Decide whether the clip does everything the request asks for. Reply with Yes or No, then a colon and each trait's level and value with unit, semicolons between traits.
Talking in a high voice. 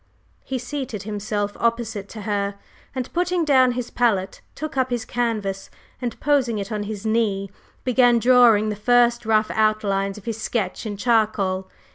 Yes: high, 220 Hz